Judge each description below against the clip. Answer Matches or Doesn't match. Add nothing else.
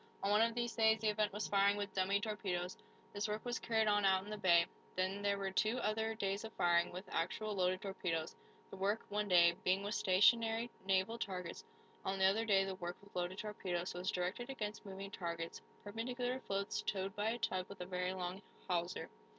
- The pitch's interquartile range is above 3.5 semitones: Doesn't match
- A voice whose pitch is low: Doesn't match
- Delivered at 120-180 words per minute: Doesn't match